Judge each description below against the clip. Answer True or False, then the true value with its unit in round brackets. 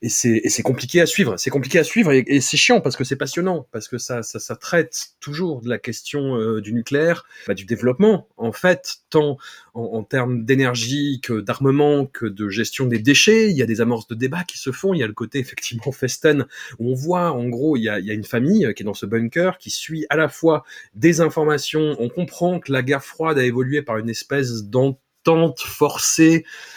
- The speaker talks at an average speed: False (235 wpm)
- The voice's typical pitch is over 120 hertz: True (135 Hz)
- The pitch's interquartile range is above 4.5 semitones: True (5.2 semitones)